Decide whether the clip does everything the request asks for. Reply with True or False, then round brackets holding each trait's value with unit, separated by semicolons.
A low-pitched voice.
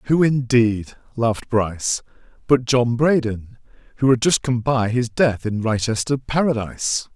True (120 Hz)